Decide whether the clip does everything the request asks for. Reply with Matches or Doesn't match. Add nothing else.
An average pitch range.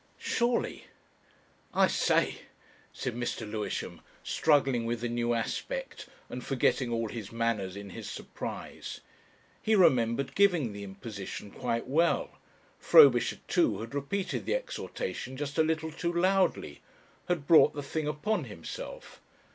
Doesn't match